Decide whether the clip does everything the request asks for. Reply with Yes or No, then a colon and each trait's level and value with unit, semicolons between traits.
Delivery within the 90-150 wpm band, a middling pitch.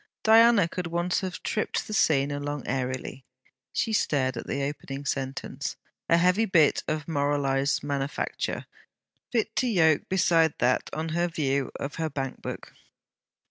Yes: average, 145 wpm; medium, 150 Hz